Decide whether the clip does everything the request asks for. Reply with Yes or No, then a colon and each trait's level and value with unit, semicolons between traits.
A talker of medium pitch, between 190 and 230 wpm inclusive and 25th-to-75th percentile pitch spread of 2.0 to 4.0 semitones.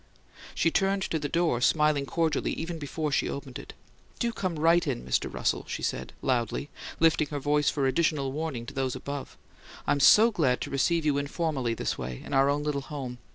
Yes: medium, 145 Hz; average, 200 wpm; average, 3.3 semitones